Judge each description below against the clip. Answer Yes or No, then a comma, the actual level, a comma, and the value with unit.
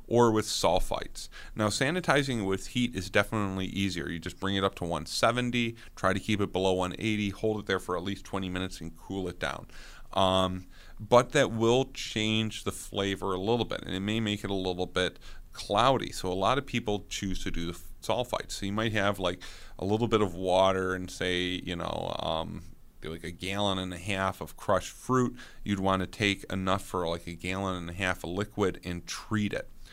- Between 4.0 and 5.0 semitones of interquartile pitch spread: No, average, 3.0 semitones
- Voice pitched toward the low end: Yes, very low, 95 Hz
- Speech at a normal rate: No, fast, 215 wpm